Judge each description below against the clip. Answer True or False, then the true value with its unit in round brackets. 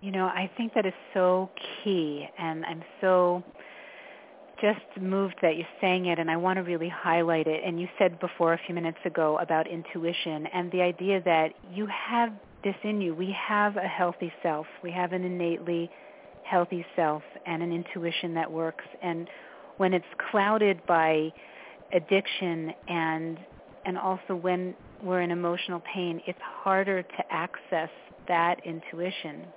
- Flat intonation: True (2.1 semitones)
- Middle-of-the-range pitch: True (180 Hz)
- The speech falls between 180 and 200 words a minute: False (160 wpm)